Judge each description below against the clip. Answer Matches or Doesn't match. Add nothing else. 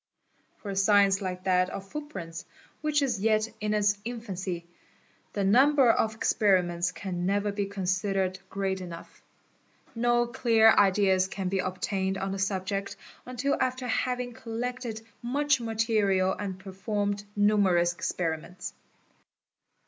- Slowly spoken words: Matches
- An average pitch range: Matches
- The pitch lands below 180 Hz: Doesn't match